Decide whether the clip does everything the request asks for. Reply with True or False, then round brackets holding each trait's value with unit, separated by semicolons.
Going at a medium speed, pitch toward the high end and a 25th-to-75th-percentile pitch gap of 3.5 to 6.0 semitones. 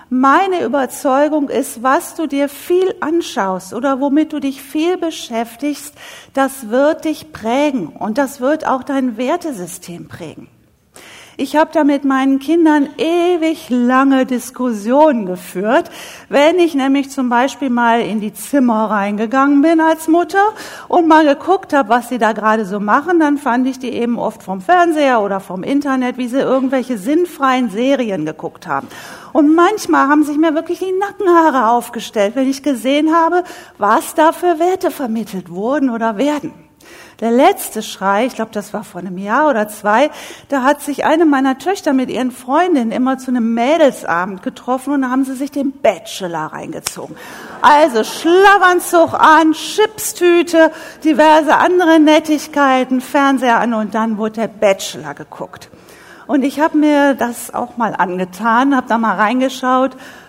True (155 wpm; 275 Hz; 4.9 semitones)